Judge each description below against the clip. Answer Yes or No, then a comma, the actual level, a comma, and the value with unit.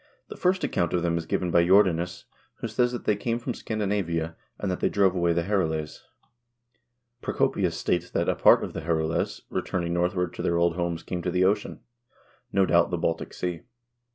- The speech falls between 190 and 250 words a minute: Yes, average, 195 wpm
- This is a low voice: Yes, very low, 90 Hz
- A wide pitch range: No, narrow, 2.6 semitones